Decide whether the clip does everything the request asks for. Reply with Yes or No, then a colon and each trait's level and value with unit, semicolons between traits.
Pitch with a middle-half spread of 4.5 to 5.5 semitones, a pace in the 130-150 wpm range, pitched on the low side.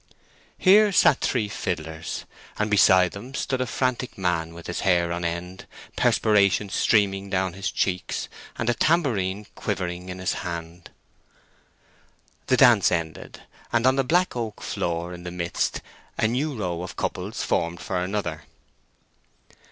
Yes: average, 4.8 semitones; average, 145 wpm; very low, 95 Hz